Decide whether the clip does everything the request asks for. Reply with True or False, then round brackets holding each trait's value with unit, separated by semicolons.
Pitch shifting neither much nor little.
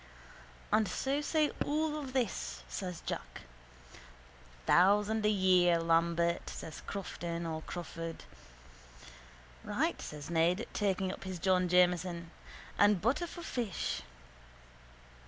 True (4.2 semitones)